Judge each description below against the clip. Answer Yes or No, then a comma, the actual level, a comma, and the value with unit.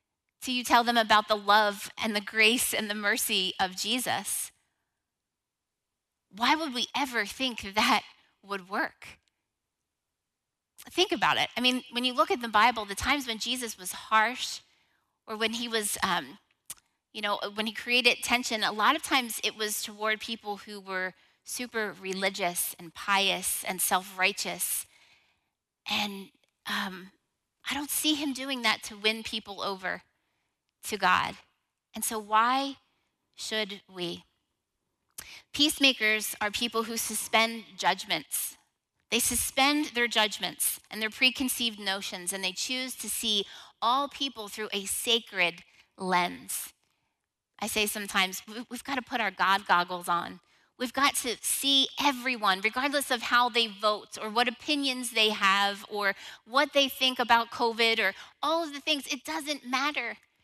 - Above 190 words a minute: No, average, 150 wpm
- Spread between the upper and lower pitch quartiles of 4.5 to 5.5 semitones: No, average, 3.8 semitones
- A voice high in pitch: Yes, high, 220 Hz